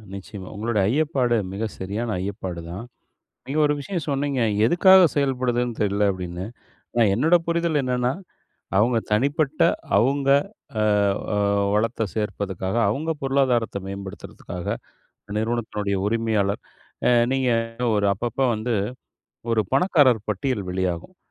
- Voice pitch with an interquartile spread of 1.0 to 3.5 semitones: No, average, 5.0 semitones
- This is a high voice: No, low, 115 Hz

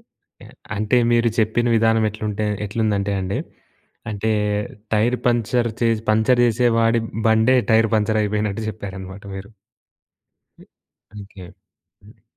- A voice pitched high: No, low, 110 Hz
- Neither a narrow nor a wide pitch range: No, narrow, 1.8 semitones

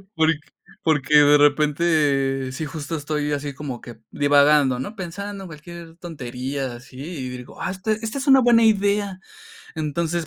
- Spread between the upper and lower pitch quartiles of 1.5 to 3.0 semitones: No, average, 3.8 semitones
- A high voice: No, medium, 150 Hz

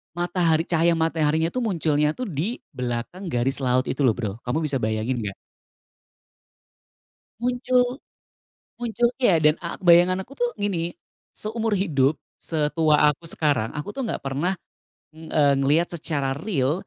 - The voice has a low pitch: No, medium, 160 Hz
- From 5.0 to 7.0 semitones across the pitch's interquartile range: Yes, wide, 5.5 semitones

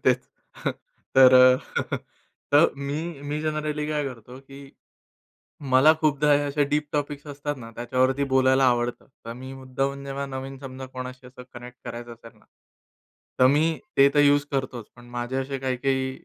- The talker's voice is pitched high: No, low, 135 Hz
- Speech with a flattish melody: Yes, narrow, 2.1 semitones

